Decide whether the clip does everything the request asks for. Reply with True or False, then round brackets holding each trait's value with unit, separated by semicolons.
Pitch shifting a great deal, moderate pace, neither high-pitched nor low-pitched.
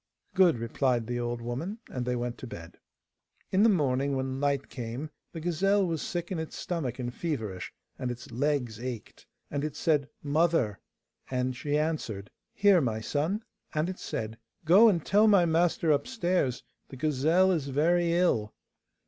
True (5.9 semitones; 165 wpm; 145 Hz)